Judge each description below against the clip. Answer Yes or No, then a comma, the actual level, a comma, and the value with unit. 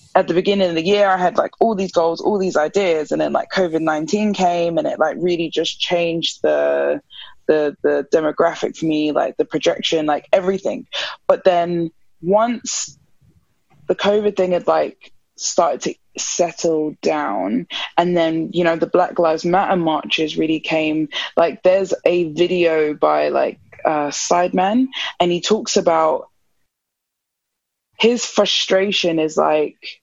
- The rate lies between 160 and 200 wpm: No, average, 150 wpm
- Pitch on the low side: No, medium, 175 Hz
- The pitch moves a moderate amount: Yes, average, 3.3 semitones